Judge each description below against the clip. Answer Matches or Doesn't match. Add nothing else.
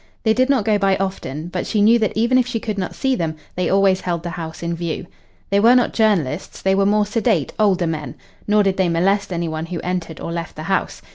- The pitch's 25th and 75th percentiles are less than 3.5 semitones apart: Doesn't match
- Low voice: Doesn't match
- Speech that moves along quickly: Matches